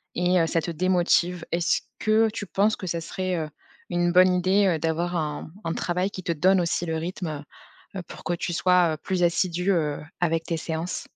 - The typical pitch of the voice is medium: Yes, medium, 175 Hz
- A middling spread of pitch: No, narrow, 2.0 semitones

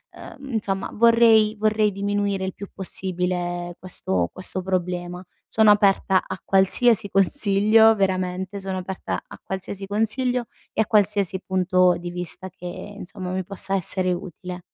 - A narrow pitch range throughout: Yes, narrow, 2.3 semitones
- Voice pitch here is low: No, high, 190 Hz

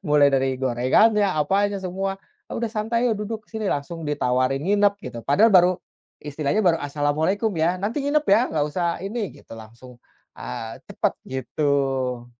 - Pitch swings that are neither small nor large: No, wide, 6.7 semitones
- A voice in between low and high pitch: Yes, medium, 170 Hz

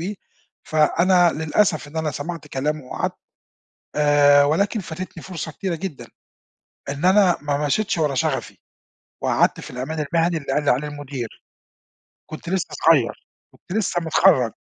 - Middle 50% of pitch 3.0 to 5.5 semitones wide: Yes, average, 3.4 semitones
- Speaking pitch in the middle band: Yes, medium, 155 Hz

